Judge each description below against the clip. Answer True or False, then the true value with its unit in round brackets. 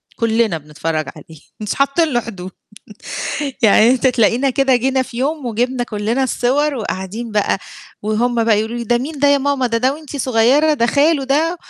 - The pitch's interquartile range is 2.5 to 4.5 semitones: True (3.8 semitones)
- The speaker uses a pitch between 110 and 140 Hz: False (245 Hz)